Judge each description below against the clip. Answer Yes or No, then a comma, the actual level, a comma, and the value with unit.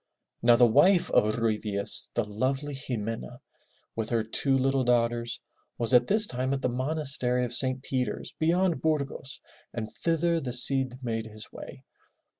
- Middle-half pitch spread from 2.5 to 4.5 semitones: Yes, average, 2.9 semitones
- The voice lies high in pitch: No, low, 125 Hz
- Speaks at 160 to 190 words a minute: Yes, average, 165 wpm